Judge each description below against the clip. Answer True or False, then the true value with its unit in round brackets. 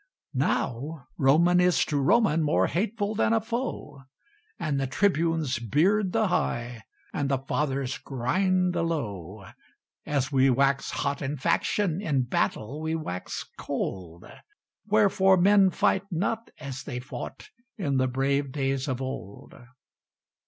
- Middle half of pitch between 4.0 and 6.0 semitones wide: True (5.6 semitones)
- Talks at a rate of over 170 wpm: False (135 wpm)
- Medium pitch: True (145 Hz)